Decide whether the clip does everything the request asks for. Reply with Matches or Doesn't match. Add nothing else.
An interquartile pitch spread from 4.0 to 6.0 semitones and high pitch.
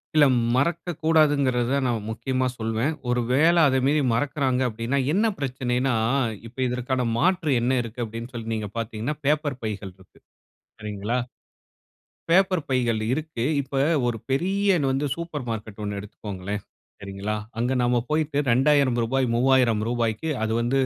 Doesn't match